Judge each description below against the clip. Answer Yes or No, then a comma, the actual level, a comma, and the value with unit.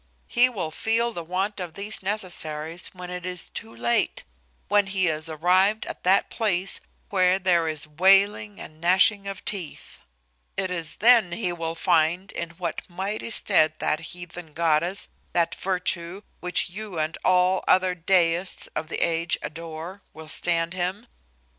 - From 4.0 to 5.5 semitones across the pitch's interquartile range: No, average, 2.7 semitones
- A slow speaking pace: No, average, 155 wpm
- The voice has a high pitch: No, medium, 180 Hz